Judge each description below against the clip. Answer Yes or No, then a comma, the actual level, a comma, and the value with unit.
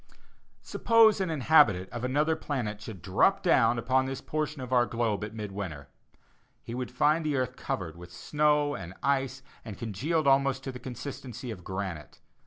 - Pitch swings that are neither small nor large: No, wide, 5.7 semitones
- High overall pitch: No, low, 125 Hz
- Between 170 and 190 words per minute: Yes, average, 175 wpm